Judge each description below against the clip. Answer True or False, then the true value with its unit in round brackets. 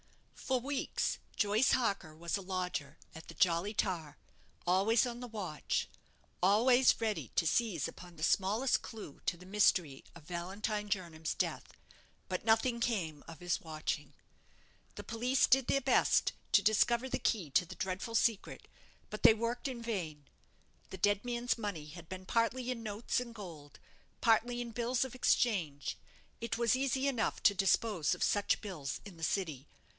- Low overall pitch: False (205 Hz)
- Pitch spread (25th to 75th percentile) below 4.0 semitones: False (5.4 semitones)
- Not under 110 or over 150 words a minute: False (165 wpm)